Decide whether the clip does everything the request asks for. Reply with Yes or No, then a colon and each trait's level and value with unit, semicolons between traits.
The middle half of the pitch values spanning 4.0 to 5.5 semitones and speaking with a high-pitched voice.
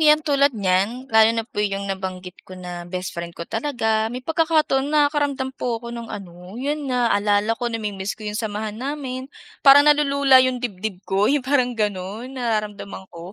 Yes: average, 5.2 semitones; high, 225 Hz